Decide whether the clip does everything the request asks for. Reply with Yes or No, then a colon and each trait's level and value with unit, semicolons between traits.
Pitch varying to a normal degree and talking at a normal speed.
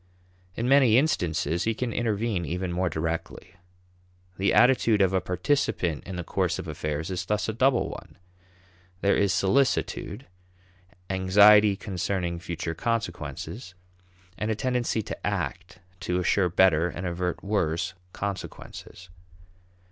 No: average, 3.9 semitones; slow, 130 wpm